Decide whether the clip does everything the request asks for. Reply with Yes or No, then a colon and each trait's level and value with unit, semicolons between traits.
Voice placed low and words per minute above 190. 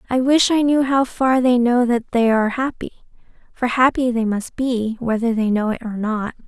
No: high, 240 Hz; fast, 205 wpm